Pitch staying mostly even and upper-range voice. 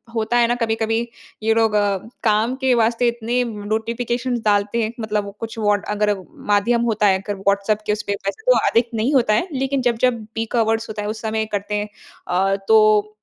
Yes: narrow, 2.0 semitones; high, 220 Hz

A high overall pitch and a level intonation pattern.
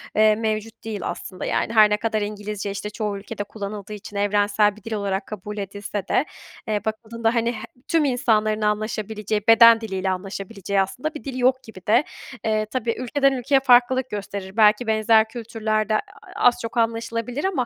Yes: high, 215 Hz; narrow, 2.0 semitones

